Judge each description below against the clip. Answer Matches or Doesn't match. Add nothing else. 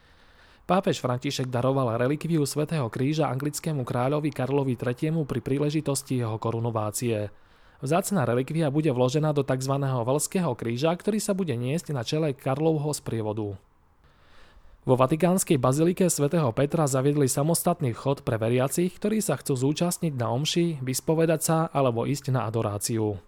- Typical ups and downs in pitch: Matches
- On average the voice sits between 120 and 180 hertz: Matches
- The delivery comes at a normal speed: Matches